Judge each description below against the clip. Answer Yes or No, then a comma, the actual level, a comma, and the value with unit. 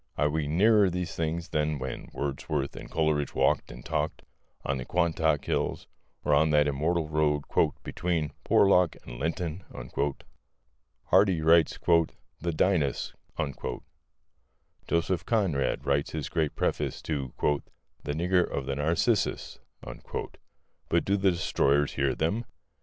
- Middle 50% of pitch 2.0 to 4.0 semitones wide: Yes, average, 3.0 semitones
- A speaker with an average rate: No, slow, 125 wpm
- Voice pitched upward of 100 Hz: No, very low, 80 Hz